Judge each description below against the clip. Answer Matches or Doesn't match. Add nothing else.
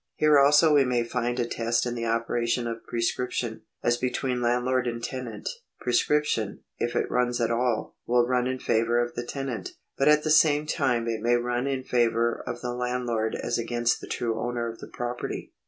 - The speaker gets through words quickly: Doesn't match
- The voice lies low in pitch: Matches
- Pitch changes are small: Matches